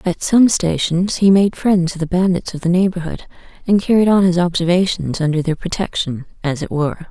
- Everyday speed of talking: Yes, average, 195 wpm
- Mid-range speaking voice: Yes, medium, 175 Hz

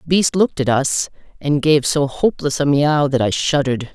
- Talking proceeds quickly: Yes, fast, 215 wpm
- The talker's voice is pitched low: No, medium, 145 Hz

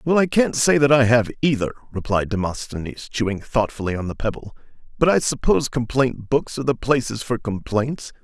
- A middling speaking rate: Yes, average, 180 wpm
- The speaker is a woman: No, male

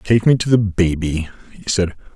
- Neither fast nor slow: Yes, average, 195 wpm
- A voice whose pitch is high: No, very low, 95 Hz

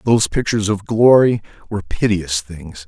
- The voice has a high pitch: No, low, 100 Hz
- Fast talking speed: No, average, 145 wpm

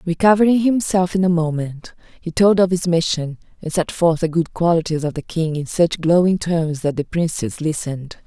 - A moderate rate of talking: Yes, average, 195 wpm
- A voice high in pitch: No, medium, 170 Hz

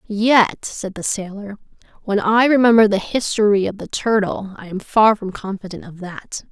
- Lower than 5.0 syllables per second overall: Yes, 4.6 syllables/s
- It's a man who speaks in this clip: No, female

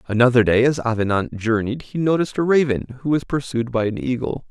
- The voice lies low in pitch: Yes, low, 125 Hz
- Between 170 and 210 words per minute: Yes, average, 200 wpm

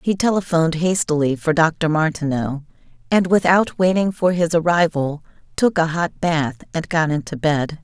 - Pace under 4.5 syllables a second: No, 4.7 syllables/s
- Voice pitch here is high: No, medium, 165 Hz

